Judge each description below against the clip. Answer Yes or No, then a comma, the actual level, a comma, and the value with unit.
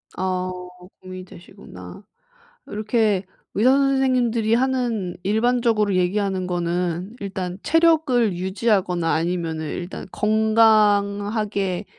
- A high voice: Yes, high, 205 Hz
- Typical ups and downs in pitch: Yes, average, 3.9 semitones